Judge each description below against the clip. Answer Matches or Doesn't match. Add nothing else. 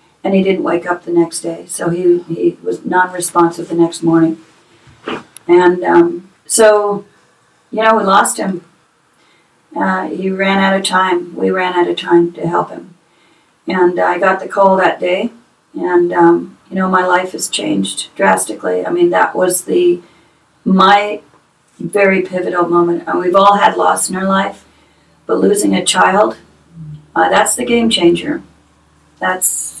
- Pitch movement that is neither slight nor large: Doesn't match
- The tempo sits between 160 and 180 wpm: Matches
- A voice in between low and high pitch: Matches